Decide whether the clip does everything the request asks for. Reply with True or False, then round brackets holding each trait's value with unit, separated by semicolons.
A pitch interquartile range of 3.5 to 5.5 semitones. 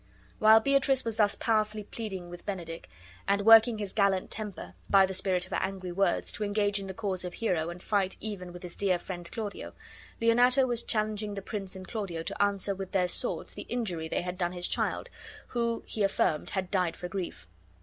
False (3.1 semitones)